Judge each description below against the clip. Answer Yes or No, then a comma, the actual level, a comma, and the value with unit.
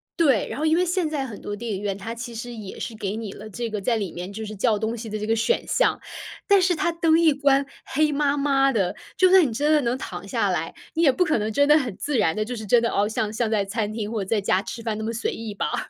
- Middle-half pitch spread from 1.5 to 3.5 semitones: No, average, 5.2 semitones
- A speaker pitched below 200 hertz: No, high, 230 Hz